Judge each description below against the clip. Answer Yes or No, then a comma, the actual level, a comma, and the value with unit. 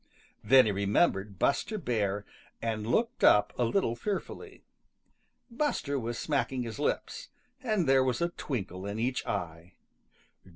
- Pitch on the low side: Yes, low, 120 Hz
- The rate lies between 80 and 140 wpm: Yes, slow, 135 wpm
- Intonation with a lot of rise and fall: Yes, wide, 6.6 semitones